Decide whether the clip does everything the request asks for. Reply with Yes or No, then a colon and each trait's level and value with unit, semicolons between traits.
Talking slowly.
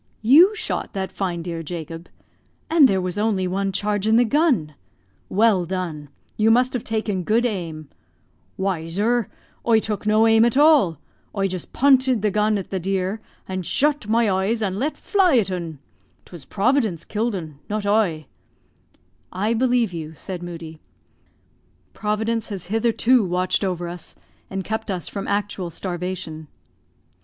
No: average, 155 wpm